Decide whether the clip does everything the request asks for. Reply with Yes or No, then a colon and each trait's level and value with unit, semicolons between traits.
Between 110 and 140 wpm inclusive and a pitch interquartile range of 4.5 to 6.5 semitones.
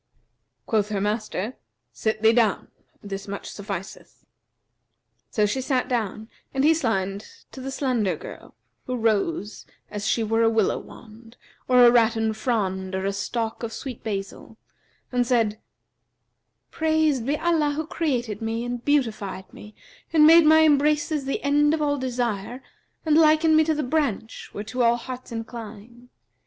No: average, 155 wpm; average, 5.0 semitones